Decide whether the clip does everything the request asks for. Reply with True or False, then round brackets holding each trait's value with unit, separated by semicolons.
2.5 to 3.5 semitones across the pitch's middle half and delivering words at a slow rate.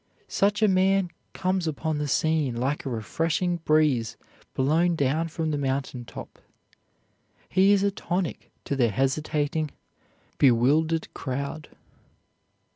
False (4.2 semitones; 120 wpm)